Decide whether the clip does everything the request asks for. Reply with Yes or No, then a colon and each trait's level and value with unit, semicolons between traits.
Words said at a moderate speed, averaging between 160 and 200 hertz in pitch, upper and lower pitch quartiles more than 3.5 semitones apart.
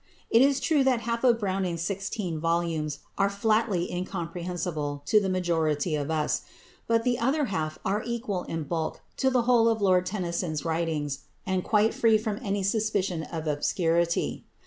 Yes: average, 165 wpm; medium, 185 Hz; average, 5.2 semitones